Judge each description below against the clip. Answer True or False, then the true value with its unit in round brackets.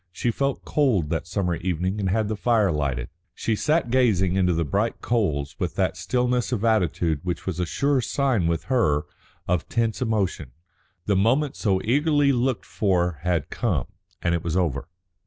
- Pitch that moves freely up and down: True (6.0 semitones)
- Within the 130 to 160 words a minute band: False (175 wpm)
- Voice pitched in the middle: False (95 Hz)